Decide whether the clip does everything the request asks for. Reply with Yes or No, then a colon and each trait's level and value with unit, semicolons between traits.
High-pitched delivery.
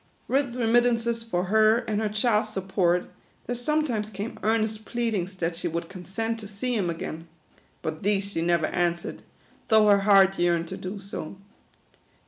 Yes: high, 205 Hz